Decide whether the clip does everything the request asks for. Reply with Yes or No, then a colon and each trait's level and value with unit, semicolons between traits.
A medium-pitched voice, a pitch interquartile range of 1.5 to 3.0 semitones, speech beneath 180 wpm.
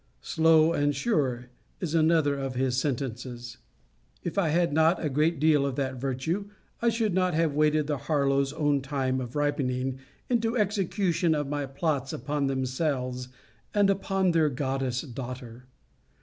No: medium, 145 Hz; average, 4.0 semitones; average, 150 wpm